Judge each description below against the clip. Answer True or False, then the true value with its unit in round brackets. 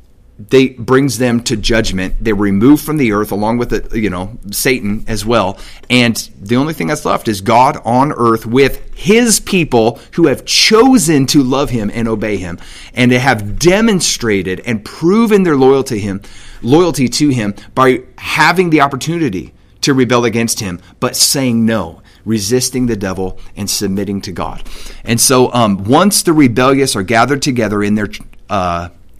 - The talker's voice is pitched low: True (115 Hz)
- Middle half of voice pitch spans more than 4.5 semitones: True (4.9 semitones)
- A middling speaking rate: True (170 wpm)